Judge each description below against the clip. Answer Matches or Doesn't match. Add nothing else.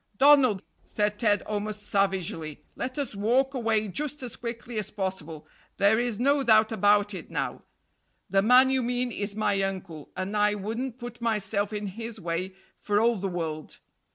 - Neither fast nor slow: Matches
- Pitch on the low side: Doesn't match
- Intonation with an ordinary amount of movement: Matches